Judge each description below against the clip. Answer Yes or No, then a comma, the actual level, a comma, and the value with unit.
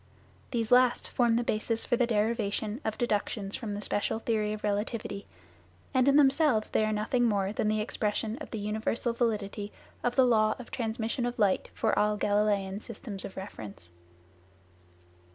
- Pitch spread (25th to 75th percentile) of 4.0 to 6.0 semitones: No, narrow, 2.4 semitones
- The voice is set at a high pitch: Yes, high, 215 Hz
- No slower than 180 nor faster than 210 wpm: No, average, 170 wpm